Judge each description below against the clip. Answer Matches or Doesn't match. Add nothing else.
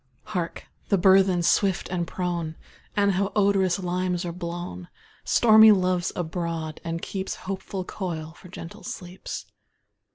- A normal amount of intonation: Doesn't match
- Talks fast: Doesn't match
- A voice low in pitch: Doesn't match